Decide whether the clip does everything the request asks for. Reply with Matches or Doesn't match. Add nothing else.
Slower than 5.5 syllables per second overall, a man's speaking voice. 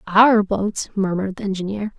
Doesn't match